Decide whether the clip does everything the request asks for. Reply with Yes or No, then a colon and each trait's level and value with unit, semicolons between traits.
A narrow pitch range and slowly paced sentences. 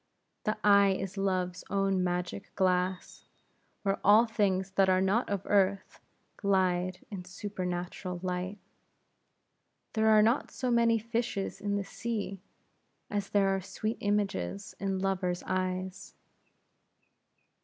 Yes: narrow, 1.9 semitones; slow, 120 wpm